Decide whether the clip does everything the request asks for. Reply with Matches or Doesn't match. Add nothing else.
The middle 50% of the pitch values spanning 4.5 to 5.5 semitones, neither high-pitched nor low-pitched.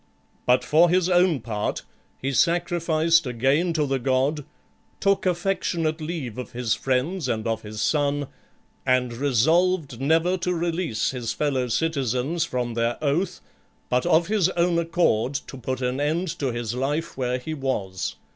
Matches